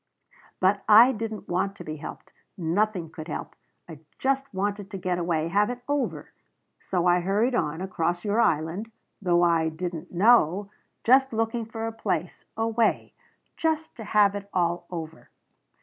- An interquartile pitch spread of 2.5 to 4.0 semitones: No, average, 4.5 semitones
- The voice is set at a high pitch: Yes, high, 195 Hz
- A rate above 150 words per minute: Yes, average, 165 wpm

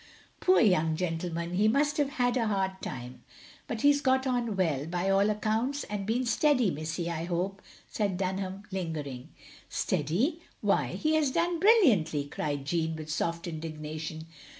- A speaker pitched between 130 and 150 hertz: No, high, 190 Hz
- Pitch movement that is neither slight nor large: No, wide, 7.2 semitones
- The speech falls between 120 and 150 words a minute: No, average, 160 wpm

